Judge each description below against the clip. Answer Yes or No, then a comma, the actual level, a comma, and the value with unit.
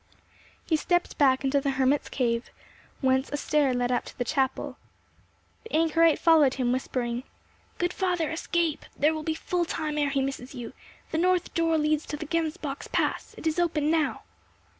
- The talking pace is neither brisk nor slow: Yes, average, 175 wpm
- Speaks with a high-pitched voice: Yes, very high, 300 Hz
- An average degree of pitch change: Yes, average, 3.6 semitones